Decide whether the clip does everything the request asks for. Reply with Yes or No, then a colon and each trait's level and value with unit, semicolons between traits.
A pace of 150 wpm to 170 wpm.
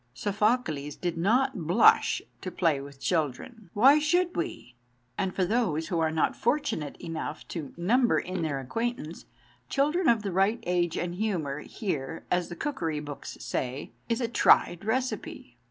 Yes: average, 155 wpm